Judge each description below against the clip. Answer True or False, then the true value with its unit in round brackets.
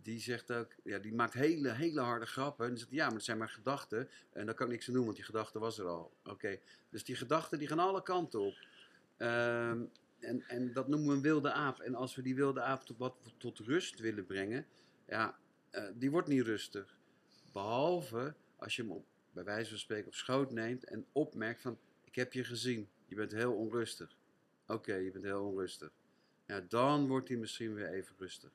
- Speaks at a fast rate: True (220 wpm)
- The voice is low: True (120 Hz)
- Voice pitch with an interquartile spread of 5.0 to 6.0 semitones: False (3.3 semitones)